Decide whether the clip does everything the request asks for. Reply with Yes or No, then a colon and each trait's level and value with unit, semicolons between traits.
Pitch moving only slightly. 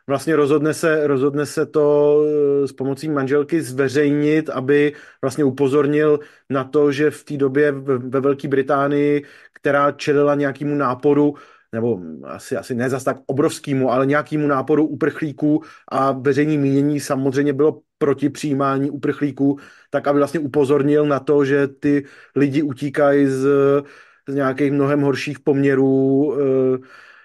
Yes: narrow, 1.1 semitones